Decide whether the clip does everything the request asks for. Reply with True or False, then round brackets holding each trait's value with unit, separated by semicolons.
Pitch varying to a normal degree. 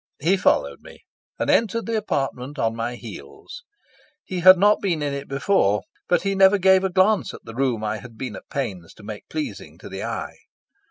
False (8.7 semitones)